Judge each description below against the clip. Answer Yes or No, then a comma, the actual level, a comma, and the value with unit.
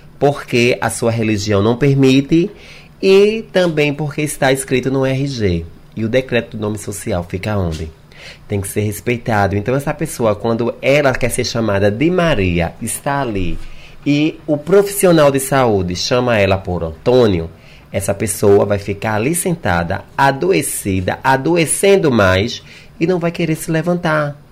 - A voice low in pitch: Yes, low, 125 Hz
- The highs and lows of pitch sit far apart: Yes, wide, 6.6 semitones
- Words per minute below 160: Yes, average, 150 wpm